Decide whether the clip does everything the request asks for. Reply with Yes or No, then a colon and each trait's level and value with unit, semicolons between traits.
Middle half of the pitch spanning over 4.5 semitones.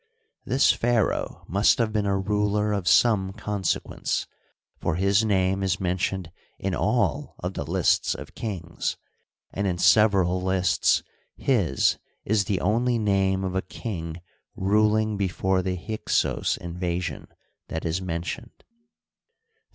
No: average, 2.7 semitones